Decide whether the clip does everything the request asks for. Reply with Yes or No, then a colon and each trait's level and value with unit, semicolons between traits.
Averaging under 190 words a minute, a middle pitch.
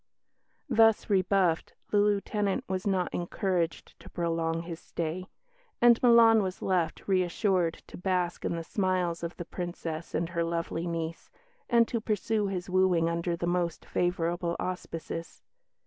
Yes: average, 145 wpm; medium, 180 Hz